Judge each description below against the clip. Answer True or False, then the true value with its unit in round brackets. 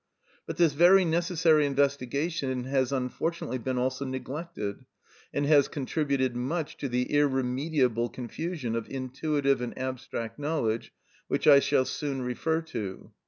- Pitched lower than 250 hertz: True (135 Hz)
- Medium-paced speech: False (130 wpm)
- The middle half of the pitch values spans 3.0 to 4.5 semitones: True (3.5 semitones)